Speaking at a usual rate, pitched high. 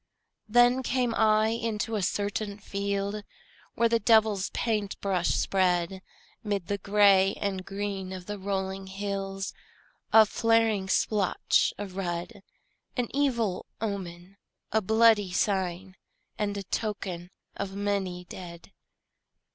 No: slow, 120 wpm; high, 200 Hz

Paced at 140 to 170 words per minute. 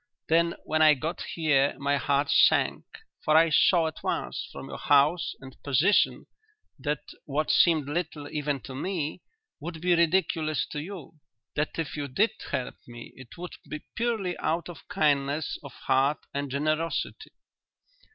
Yes: average, 155 wpm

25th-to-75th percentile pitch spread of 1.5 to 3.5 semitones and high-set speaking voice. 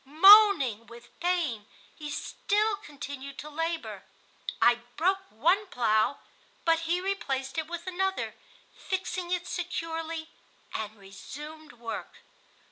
No: average, 5.3 semitones; very high, 320 Hz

